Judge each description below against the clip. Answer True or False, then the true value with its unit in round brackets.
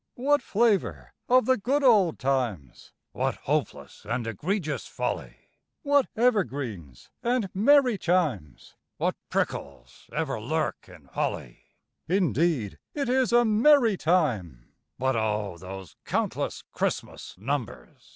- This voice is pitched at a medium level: True (155 Hz)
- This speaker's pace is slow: True (120 wpm)